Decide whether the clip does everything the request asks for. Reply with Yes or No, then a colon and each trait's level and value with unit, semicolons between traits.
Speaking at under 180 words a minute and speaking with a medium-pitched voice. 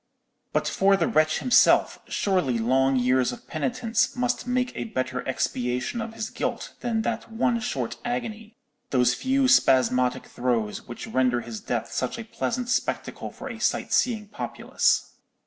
Yes: average, 150 wpm; medium, 155 Hz